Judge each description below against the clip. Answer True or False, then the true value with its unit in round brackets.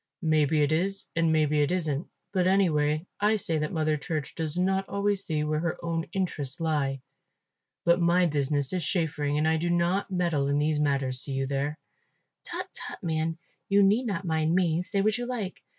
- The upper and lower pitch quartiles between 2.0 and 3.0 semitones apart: False (3.5 semitones)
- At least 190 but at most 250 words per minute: True (195 wpm)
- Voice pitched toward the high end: False (160 Hz)